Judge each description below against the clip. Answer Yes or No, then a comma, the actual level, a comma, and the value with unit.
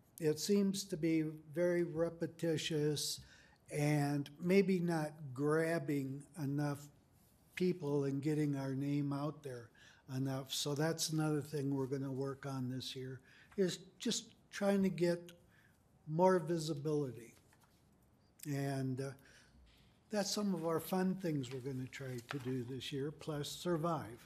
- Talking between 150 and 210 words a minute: No, slow, 135 wpm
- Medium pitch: Yes, medium, 150 Hz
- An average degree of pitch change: Yes, average, 3.7 semitones